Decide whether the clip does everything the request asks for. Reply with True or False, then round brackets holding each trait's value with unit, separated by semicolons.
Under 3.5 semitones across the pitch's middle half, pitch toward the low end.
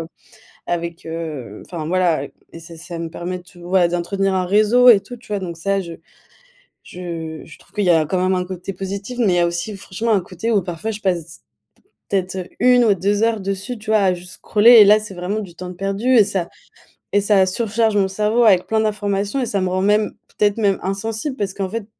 False (3.1 semitones; 195 Hz)